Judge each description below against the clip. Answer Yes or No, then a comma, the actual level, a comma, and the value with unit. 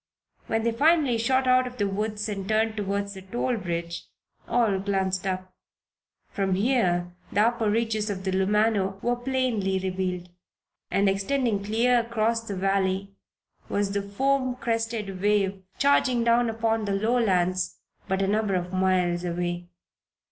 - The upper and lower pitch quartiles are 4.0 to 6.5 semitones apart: No, average, 3.4 semitones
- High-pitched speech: Yes, high, 205 Hz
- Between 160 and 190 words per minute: No, average, 150 wpm